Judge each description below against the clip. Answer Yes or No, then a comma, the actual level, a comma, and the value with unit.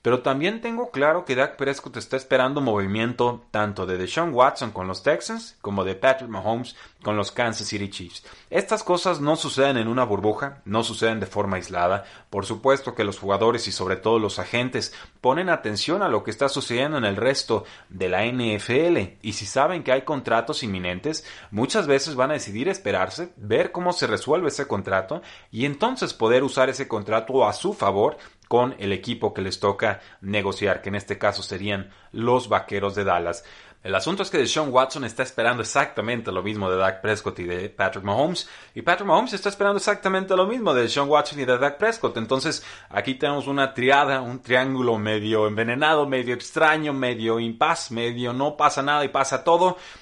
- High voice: No, low, 120 Hz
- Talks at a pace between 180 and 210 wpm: Yes, fast, 190 wpm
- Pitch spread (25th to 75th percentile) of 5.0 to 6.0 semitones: Yes, wide, 5.4 semitones